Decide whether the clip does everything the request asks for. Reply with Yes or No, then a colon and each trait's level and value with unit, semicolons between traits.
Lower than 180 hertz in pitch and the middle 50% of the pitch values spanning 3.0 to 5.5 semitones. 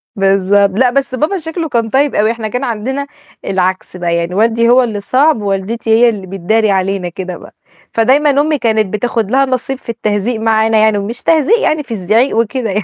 No: high, 225 Hz; average, 4.4 semitones